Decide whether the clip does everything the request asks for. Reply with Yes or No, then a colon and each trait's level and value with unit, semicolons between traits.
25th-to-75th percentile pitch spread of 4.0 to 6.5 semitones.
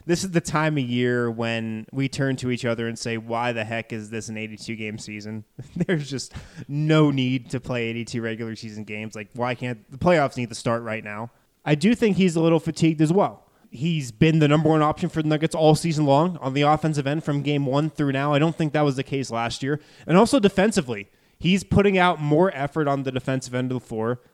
Yes: average, 5.2 semitones